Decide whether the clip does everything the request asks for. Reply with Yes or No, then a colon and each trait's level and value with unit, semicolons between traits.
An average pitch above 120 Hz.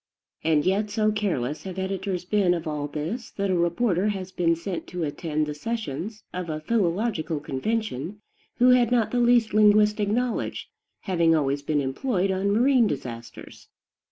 Yes: high, 190 Hz